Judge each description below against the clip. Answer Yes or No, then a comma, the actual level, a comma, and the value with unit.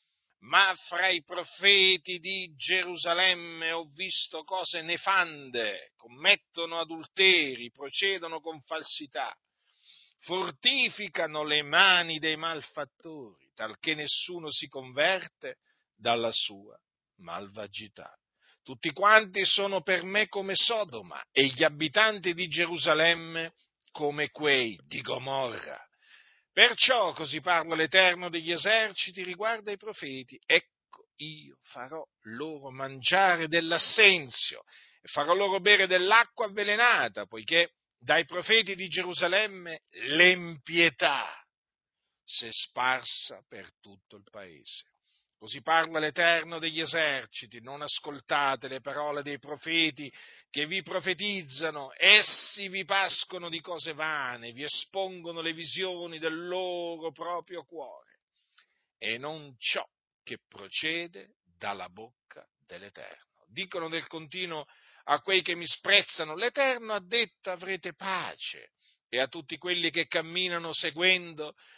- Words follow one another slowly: Yes, slow, 110 wpm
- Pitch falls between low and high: Yes, medium, 165 Hz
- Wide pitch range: No, average, 3.9 semitones